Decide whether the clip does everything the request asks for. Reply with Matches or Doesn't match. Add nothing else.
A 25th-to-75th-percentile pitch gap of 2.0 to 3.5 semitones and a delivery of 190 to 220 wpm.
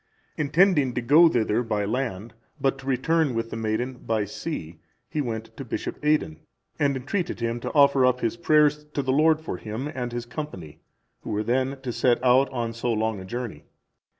Doesn't match